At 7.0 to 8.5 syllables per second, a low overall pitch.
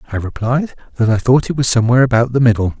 Yes: 7.4 syllables/s; low, 120 Hz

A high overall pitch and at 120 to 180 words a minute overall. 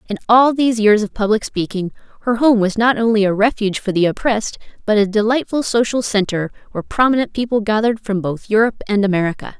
No: high, 215 Hz; average, 195 wpm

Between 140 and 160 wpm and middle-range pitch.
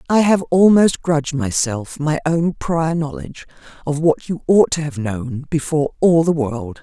No: average, 175 wpm; medium, 150 Hz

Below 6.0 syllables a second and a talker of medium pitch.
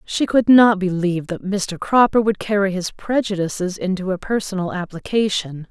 No: 5.0 syllables/s; high, 195 Hz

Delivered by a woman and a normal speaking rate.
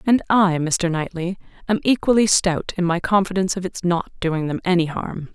Yes: female; average, 190 wpm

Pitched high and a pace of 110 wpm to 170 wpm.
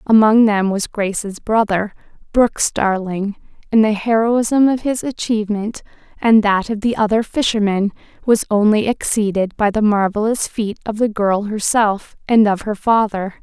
Yes: high, 215 Hz; average, 150 wpm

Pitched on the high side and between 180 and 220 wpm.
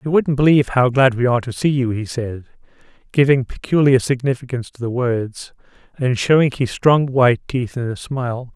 No: low, 130 Hz; average, 190 wpm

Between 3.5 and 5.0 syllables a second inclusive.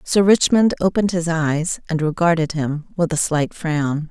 Yes: 4.5 syllables/s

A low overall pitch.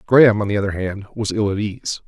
Yes: low, 105 Hz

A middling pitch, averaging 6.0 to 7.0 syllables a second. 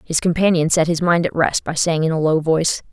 No: medium, 165 Hz; 5.8 syllables/s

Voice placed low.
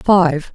No: medium, 175 Hz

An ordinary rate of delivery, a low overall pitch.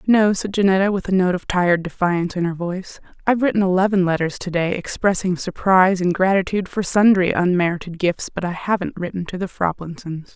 No: average, 190 wpm; medium, 185 Hz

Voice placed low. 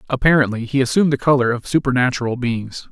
Yes: low, 130 Hz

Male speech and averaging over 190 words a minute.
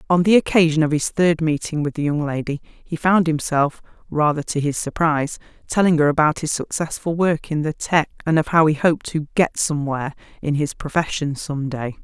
No: female; average, 200 wpm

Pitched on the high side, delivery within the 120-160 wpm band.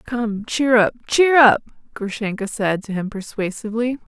Yes: high, 225 Hz; average, 145 wpm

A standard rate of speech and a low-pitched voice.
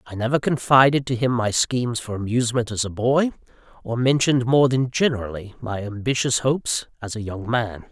Yes: average, 180 wpm; low, 120 Hz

